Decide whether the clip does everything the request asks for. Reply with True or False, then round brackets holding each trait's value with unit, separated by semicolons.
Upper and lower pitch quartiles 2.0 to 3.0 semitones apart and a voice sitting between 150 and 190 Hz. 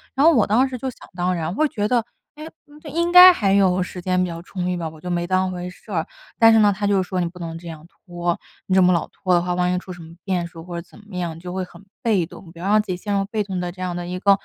True (2.6 semitones; 185 Hz)